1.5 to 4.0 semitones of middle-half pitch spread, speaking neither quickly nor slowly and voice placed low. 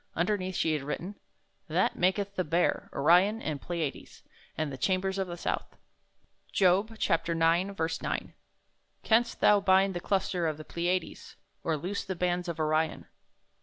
No: average, 2.9 semitones; average, 155 wpm; medium, 180 Hz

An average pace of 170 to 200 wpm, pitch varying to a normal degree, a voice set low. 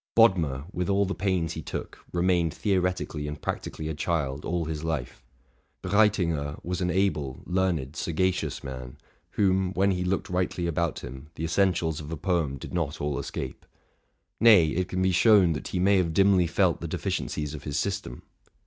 Yes: average, 180 wpm; average, 3.7 semitones; very low, 85 Hz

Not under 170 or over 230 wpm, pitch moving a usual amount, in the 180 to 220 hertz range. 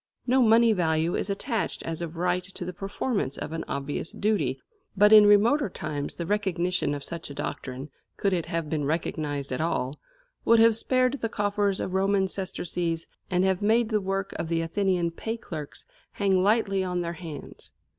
Yes: average, 185 wpm; average, 4.1 semitones; medium, 185 Hz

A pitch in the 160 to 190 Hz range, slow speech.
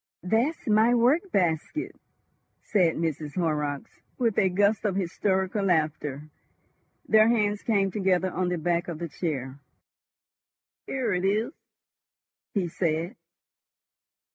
Yes: medium, 185 Hz; slow, 115 wpm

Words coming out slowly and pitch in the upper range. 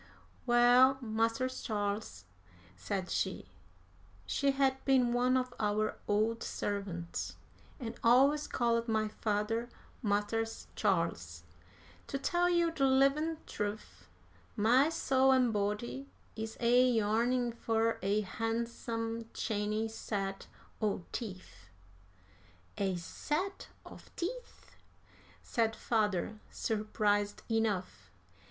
Yes: slow, 100 wpm; high, 225 Hz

